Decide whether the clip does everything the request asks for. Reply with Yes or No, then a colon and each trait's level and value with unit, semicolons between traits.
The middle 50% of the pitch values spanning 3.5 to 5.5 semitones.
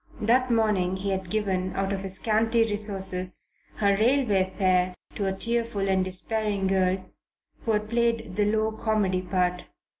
No: average, 2.7 semitones